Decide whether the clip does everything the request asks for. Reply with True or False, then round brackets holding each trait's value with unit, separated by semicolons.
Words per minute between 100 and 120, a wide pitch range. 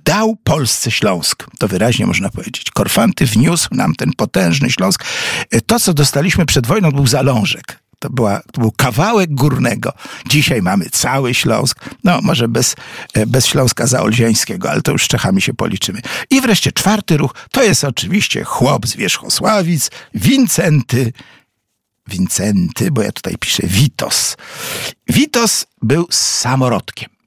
False (140 wpm; 7.4 semitones)